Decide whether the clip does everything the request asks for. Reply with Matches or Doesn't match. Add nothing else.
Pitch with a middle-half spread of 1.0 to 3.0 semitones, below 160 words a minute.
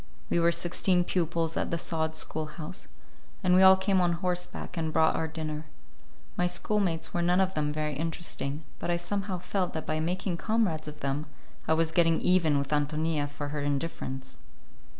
Doesn't match